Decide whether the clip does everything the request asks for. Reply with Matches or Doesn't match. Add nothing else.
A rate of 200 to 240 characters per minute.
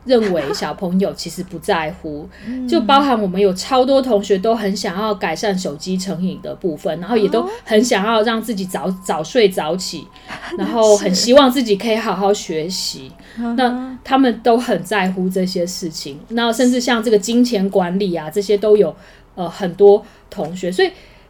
Doesn't match